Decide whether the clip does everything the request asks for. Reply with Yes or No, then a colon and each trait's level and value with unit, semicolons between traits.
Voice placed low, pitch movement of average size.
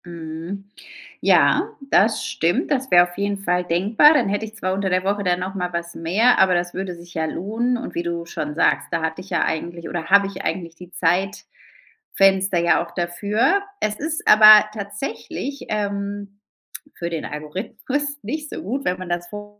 No: high, 190 Hz; average, 3.4 semitones